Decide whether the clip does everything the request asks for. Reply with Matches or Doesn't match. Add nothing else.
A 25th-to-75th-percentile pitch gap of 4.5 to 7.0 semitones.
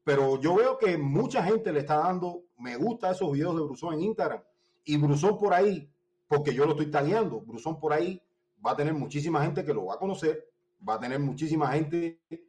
Doesn't match